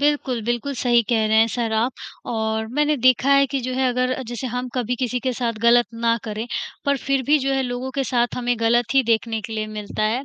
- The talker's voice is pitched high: Yes, high, 245 Hz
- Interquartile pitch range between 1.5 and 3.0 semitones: Yes, narrow, 2.5 semitones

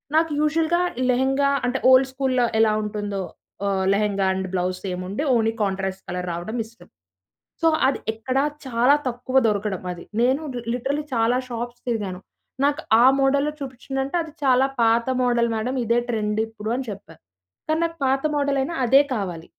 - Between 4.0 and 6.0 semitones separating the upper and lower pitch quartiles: Yes, average, 4.6 semitones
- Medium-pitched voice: No, high, 240 Hz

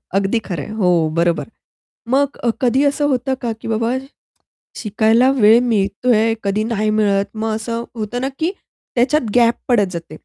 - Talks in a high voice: Yes, high, 225 Hz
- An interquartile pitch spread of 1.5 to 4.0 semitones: Yes, average, 3.3 semitones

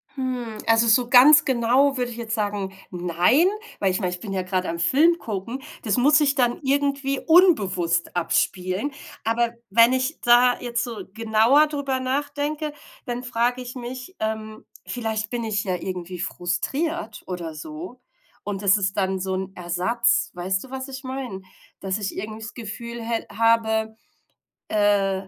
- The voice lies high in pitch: Yes, high, 230 Hz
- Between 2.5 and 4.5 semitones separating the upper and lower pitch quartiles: No, average, 5.1 semitones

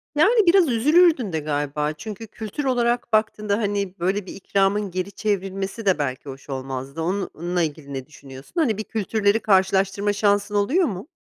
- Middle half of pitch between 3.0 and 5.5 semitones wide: Yes, average, 5.0 semitones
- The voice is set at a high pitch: Yes, high, 200 Hz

